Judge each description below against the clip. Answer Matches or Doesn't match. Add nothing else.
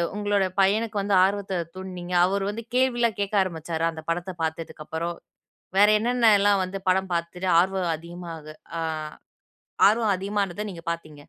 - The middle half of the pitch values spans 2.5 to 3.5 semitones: Matches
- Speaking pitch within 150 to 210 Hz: Matches